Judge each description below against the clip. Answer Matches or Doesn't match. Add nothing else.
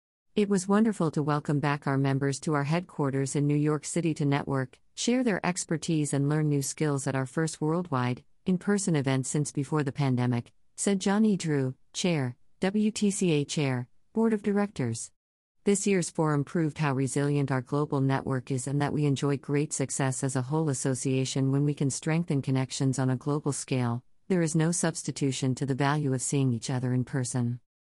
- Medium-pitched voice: Matches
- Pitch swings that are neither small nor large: Matches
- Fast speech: Doesn't match